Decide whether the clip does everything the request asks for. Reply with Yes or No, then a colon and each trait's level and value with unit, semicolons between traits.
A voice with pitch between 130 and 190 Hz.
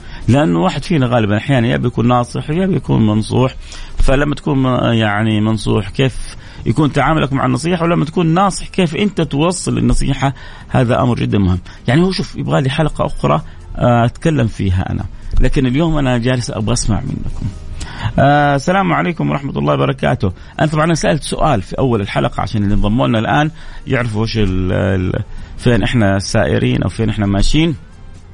No: low, 120 Hz